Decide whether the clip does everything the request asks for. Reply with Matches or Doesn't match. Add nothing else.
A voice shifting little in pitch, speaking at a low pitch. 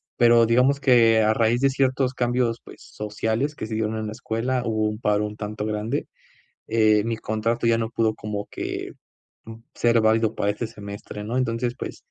Matches